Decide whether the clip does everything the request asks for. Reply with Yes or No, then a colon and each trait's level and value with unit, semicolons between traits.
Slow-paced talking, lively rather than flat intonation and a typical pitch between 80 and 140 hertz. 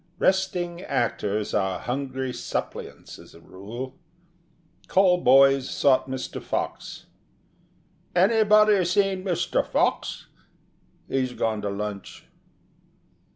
Yes: slow, 95 wpm; wide, 8.4 semitones; low, 135 Hz